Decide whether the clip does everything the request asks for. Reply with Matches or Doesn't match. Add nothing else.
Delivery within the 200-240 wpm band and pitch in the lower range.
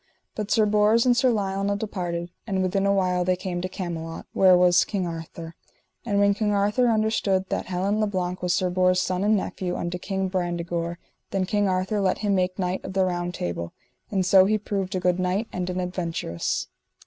Doesn't match